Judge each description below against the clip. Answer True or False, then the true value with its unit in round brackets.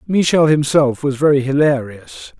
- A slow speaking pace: True (125 wpm)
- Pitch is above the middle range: False (135 Hz)